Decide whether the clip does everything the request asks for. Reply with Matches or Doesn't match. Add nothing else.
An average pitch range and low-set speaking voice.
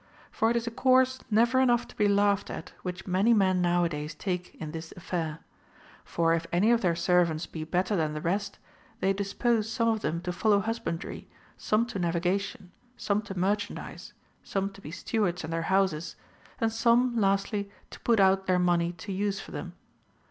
Doesn't match